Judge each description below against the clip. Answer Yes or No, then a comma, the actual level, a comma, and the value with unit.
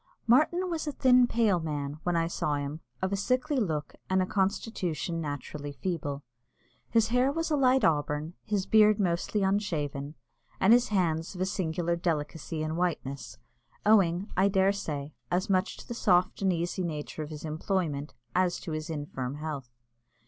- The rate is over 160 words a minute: Yes, average, 170 wpm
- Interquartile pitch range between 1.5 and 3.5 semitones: No, average, 5.1 semitones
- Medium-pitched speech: Yes, medium, 175 Hz